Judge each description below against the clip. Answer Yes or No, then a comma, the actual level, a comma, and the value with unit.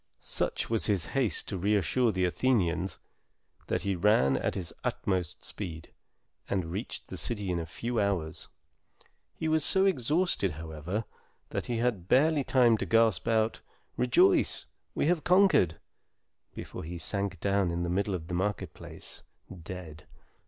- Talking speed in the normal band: Yes, average, 150 wpm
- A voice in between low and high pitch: No, low, 100 Hz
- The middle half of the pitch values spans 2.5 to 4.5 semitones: No, average, 5.3 semitones